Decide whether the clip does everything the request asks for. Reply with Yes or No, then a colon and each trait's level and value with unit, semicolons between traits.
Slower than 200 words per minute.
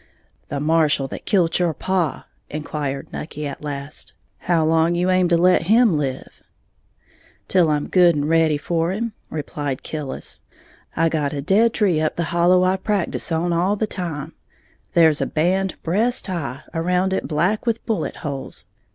Yes: average, 165 wpm